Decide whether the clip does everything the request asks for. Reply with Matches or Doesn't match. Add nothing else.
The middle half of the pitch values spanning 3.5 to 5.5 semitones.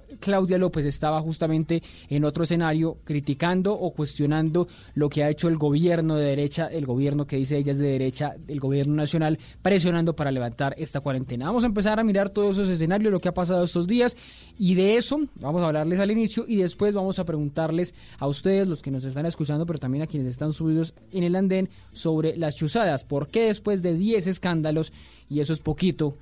Matches